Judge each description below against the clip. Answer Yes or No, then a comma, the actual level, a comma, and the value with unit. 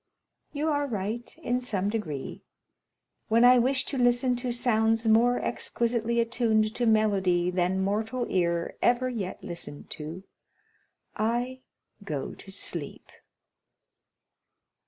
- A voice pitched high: Yes, high, 225 Hz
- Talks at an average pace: No, slow, 120 wpm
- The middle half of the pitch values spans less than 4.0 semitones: No, average, 4.3 semitones